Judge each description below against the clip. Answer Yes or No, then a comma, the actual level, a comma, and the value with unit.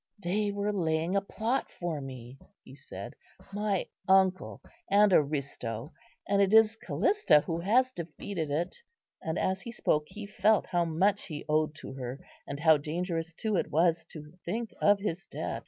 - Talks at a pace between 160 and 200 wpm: Yes, average, 170 wpm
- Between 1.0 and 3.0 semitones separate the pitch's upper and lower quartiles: No, average, 4.8 semitones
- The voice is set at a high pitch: No, medium, 175 Hz